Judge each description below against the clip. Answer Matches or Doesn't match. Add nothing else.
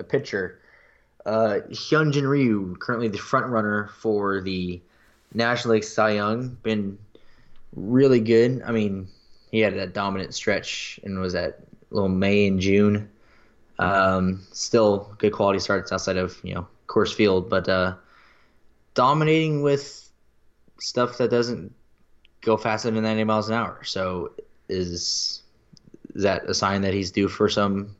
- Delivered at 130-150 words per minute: Matches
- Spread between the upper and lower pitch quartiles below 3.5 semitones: Matches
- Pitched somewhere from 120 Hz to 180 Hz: Doesn't match